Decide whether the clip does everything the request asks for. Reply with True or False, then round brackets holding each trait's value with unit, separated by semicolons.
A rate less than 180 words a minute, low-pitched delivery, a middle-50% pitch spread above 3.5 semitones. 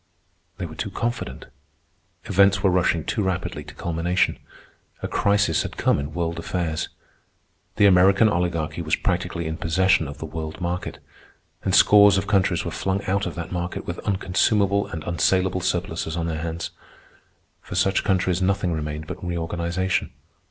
False (160 wpm; 90 Hz; 2.7 semitones)